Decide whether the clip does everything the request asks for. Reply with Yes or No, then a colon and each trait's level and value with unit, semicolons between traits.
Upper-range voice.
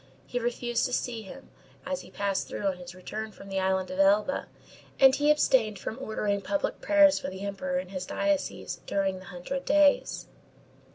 Yes: high, 215 Hz